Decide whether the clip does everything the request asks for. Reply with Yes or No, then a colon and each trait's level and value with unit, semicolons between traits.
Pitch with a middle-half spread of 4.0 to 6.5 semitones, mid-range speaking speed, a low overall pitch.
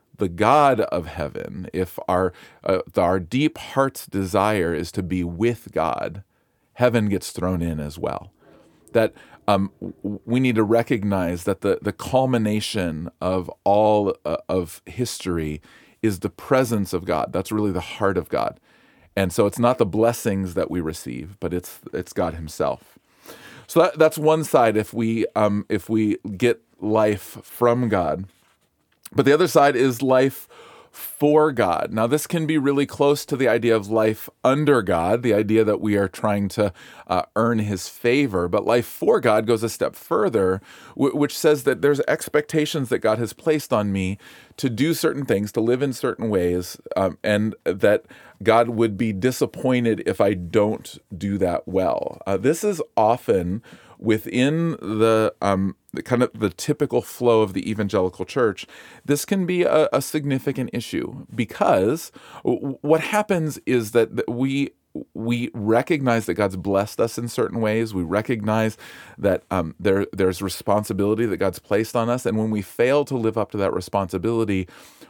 Yes: average, 4.4 semitones; average, 170 wpm; low, 110 Hz